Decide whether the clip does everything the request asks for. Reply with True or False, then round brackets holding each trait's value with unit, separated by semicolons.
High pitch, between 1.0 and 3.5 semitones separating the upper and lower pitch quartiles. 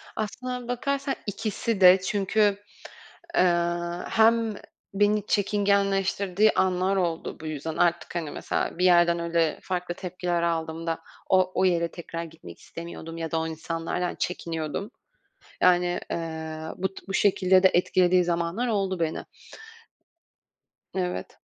False (180 Hz; 2.9 semitones)